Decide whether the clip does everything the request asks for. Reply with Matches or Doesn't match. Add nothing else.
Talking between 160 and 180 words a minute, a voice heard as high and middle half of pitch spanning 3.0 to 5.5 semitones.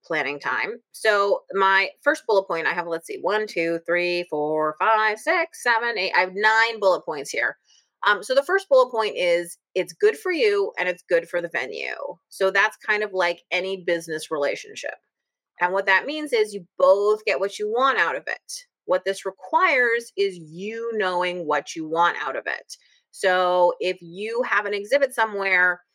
Doesn't match